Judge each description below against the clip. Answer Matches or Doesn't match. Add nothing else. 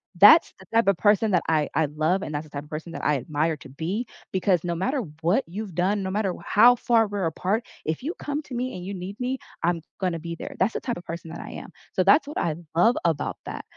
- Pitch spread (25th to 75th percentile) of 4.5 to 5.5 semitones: Matches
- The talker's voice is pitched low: Doesn't match